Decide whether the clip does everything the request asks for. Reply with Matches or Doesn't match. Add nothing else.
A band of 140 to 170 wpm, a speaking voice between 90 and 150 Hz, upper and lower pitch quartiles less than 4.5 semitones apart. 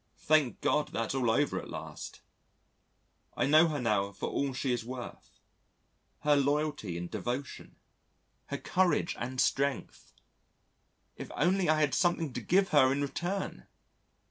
Matches